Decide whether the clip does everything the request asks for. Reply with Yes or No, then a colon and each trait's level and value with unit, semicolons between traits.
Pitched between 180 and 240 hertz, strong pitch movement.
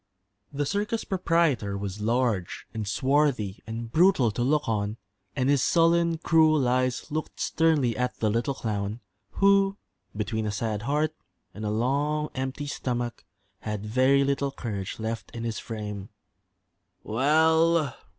No: low, 130 Hz; wide, 5.7 semitones